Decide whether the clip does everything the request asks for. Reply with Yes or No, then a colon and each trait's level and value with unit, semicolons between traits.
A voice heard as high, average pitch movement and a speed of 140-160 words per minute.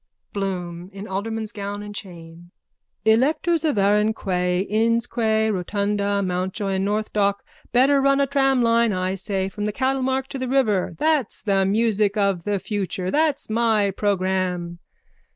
Yes: high, 205 Hz; average, 3.4 semitones; average, 150 wpm